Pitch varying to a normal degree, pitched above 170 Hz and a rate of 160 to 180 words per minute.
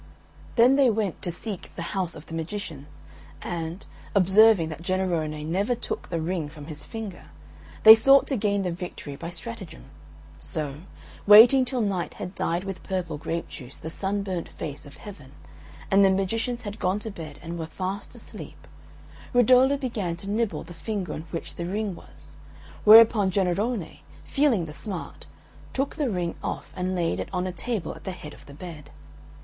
Yes: average, 4.6 semitones; medium, 185 Hz; average, 175 wpm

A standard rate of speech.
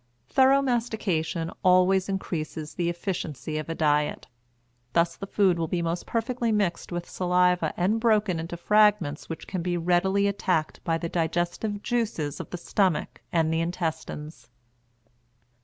Yes: average, 145 wpm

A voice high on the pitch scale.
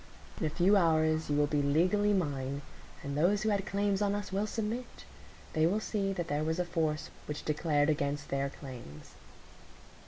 No: medium, 160 Hz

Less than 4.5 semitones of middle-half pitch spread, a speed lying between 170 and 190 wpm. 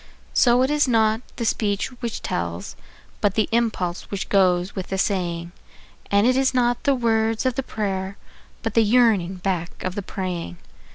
Yes: average, 3.9 semitones; average, 175 wpm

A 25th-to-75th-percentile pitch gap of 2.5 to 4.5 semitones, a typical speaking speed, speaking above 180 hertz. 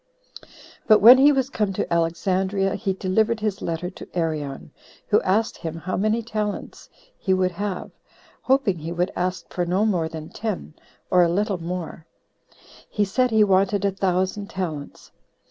Yes: average, 3.4 semitones; average, 165 wpm; high, 190 Hz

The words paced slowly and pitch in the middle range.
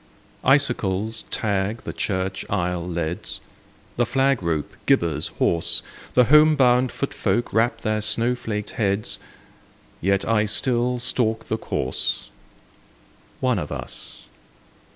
No: slow, 120 wpm; low, 110 Hz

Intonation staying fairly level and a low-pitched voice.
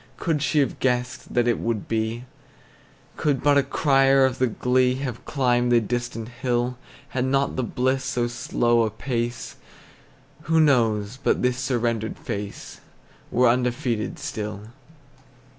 Yes: narrow, 2.0 semitones; low, 125 Hz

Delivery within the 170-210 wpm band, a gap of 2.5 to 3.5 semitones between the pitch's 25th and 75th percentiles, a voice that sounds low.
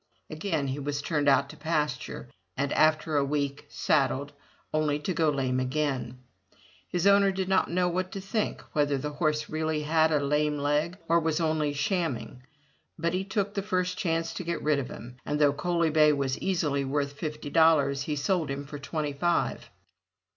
No: average, 185 wpm; average, 3.0 semitones; medium, 150 Hz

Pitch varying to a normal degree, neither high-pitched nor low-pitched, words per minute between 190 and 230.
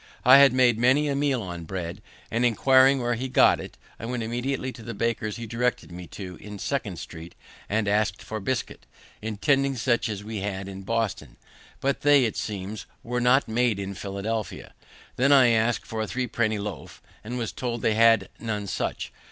No: average, 3.5 semitones; low, 115 Hz; average, 195 wpm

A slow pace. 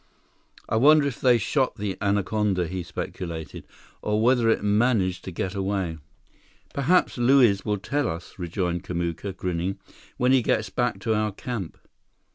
No: average, 150 wpm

